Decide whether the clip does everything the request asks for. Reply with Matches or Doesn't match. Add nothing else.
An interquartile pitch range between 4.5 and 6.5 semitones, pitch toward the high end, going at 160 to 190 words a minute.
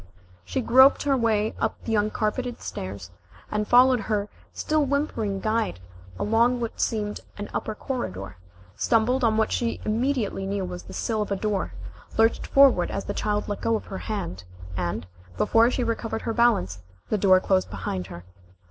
Doesn't match